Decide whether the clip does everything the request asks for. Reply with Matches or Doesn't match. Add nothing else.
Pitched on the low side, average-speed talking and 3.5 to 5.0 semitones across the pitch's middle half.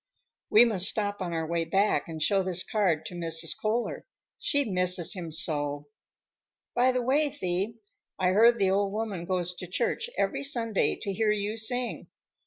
Doesn't match